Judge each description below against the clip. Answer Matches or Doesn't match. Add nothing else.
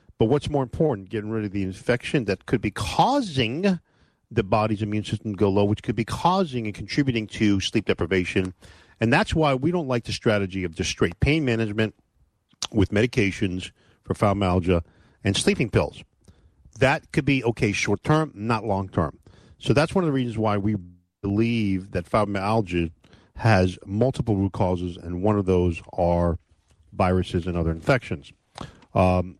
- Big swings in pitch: Doesn't match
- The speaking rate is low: Doesn't match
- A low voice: Matches